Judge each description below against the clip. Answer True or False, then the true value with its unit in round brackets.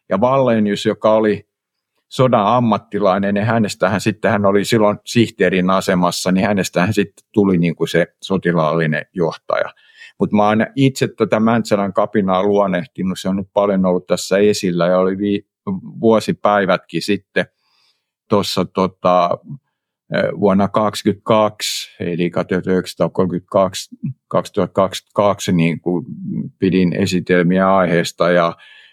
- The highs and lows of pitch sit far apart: False (2.8 semitones)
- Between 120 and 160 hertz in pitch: False (100 Hz)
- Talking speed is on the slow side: False (120 wpm)